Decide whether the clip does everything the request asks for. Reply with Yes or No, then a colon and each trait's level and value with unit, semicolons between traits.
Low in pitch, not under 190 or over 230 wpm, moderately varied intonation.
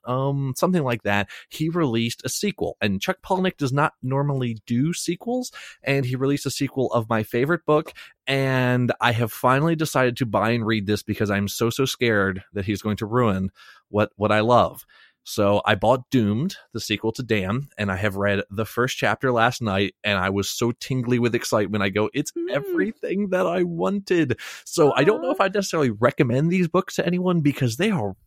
No: low, 125 Hz; average, 200 wpm; wide, 6.0 semitones